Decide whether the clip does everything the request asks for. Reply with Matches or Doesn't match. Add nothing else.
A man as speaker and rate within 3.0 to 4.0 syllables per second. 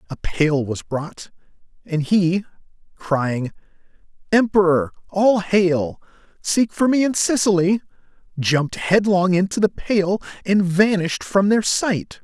Matches